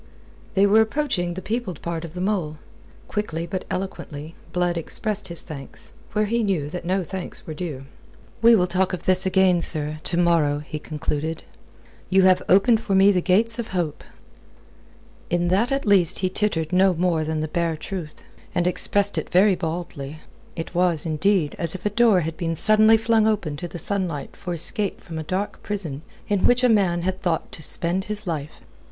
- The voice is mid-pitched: Yes, medium, 180 Hz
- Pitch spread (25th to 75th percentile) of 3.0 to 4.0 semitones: Yes, average, 3.7 semitones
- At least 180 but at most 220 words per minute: Yes, average, 190 wpm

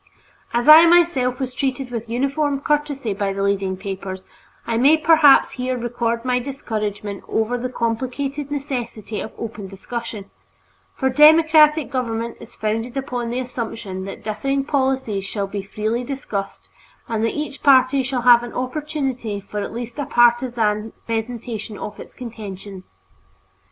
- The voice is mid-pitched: No, high, 240 Hz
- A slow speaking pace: No, average, 145 wpm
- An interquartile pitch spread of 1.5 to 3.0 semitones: No, average, 4.0 semitones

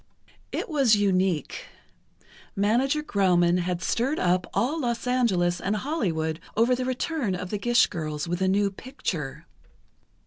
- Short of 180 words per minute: Yes, average, 140 wpm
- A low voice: No, high, 200 Hz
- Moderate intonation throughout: No, wide, 5.9 semitones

